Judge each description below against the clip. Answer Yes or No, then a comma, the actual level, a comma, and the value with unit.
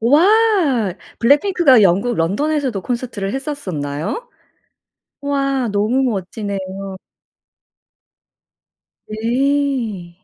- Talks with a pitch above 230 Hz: Yes, high, 240 Hz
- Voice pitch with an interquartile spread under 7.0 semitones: Yes, wide, 6.4 semitones